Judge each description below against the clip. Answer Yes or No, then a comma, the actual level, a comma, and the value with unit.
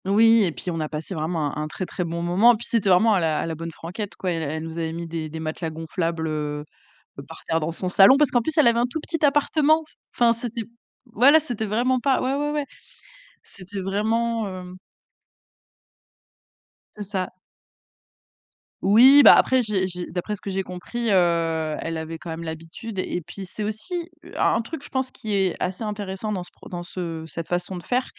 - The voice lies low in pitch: No, high, 190 Hz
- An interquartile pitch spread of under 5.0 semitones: No, wide, 5.8 semitones